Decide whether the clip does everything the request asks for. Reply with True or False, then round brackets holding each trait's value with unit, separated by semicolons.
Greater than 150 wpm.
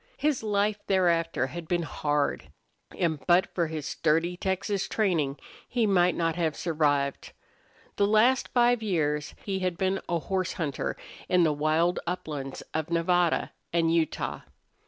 False (145 wpm)